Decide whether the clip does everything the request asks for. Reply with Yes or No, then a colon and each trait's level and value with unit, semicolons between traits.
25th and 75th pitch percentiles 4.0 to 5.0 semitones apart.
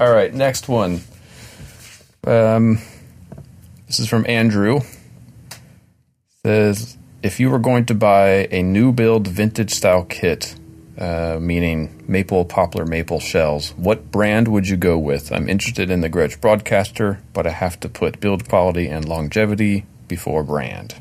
Yes: average, 4.5 semitones